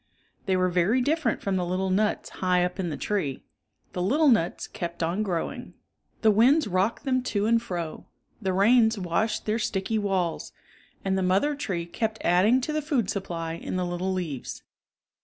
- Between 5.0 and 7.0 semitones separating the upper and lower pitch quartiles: No, average, 3.9 semitones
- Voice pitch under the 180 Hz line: No, high, 190 Hz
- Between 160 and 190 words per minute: Yes, average, 180 wpm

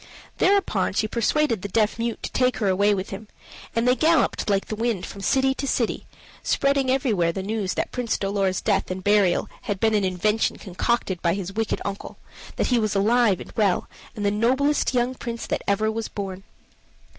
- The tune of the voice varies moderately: Yes, average, 3.5 semitones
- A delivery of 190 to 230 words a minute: Yes, average, 195 wpm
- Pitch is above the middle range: Yes, high, 215 Hz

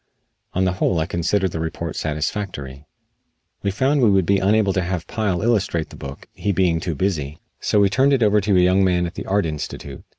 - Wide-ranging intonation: No, average, 3.6 semitones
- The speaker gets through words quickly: Yes, fast, 220 wpm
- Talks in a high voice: No, very low, 95 Hz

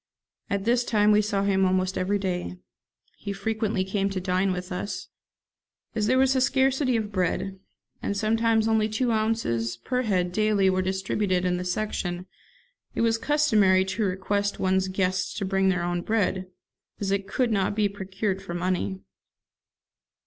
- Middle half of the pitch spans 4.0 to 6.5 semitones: No, narrow, 2.6 semitones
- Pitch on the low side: No, high, 195 Hz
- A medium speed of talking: Yes, average, 165 wpm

